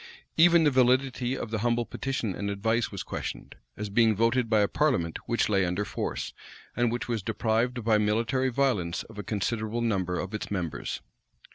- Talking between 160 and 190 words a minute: Yes, average, 180 wpm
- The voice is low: Yes, low, 115 Hz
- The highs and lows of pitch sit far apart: No, average, 3.2 semitones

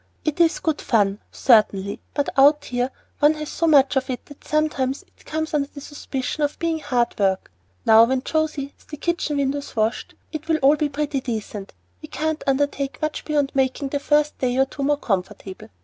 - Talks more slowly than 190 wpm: No, average, 195 wpm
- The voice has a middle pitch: No, very high, 280 Hz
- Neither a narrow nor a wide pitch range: Yes, average, 3.1 semitones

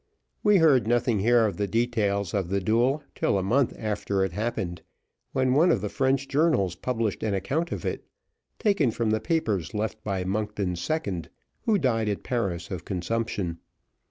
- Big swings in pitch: No, average, 4.7 semitones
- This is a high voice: No, low, 110 Hz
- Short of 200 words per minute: Yes, average, 175 wpm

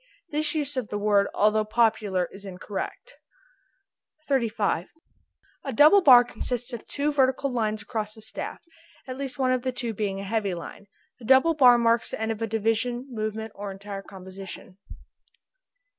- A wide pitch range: No, average, 3.8 semitones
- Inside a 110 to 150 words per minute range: No, average, 165 wpm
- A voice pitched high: Yes, high, 225 Hz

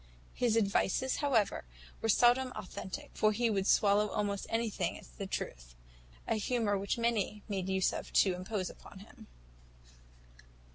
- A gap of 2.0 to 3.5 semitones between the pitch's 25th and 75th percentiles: Yes, average, 2.9 semitones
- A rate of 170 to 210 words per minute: No, average, 145 wpm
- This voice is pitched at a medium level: No, high, 210 Hz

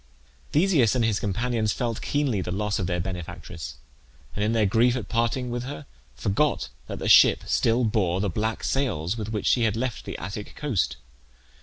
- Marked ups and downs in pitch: No, average, 3.7 semitones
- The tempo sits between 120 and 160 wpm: No, average, 185 wpm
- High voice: No, low, 110 Hz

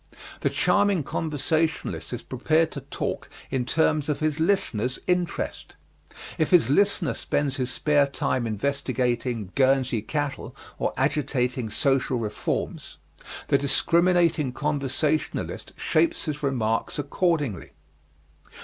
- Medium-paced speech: No, slow, 110 wpm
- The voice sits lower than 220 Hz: Yes, medium, 140 Hz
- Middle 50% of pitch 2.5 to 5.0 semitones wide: Yes, average, 3.7 semitones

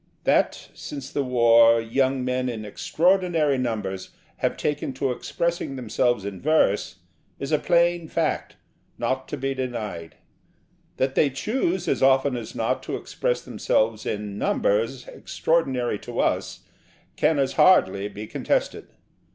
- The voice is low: Yes, low, 130 Hz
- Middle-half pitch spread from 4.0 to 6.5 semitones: Yes, average, 4.5 semitones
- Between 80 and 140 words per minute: Yes, slow, 135 wpm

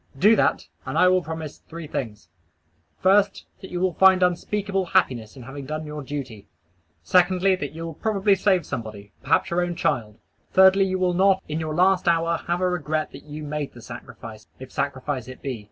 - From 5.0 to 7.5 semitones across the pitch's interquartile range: Yes, wide, 5.4 semitones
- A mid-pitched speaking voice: Yes, medium, 165 Hz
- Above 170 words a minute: Yes, average, 190 wpm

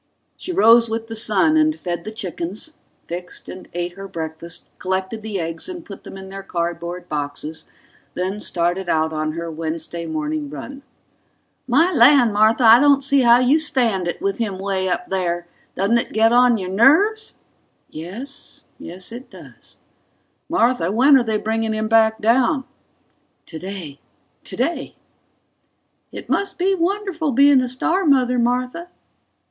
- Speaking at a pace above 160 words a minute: No, average, 155 wpm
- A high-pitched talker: Yes, high, 220 Hz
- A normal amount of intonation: No, wide, 7.0 semitones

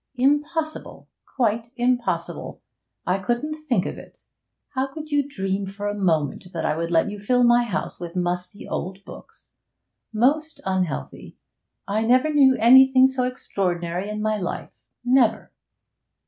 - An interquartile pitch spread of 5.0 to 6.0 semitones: Yes, wide, 5.6 semitones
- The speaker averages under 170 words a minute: Yes, average, 145 wpm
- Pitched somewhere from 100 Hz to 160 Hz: No, high, 225 Hz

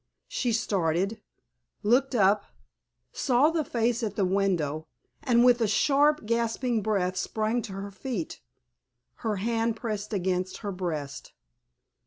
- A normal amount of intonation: Yes, average, 3.9 semitones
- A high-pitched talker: Yes, high, 215 Hz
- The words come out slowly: Yes, slow, 130 wpm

